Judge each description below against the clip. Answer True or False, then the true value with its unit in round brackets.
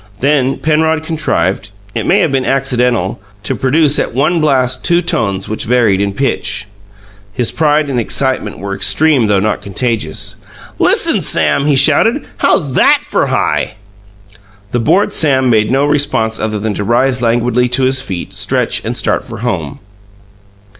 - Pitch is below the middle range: True (130 Hz)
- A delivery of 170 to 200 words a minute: False (160 wpm)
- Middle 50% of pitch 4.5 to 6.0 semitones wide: True (5.1 semitones)